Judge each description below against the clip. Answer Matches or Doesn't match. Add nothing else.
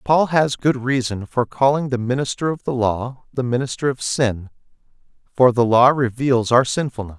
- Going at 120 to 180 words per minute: Matches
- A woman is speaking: Doesn't match